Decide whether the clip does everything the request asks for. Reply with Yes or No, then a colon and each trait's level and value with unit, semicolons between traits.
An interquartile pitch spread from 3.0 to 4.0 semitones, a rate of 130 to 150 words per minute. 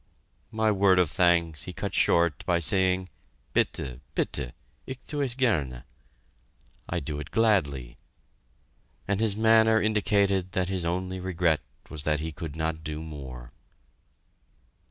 No: average, 4.8 semitones; slow, 135 wpm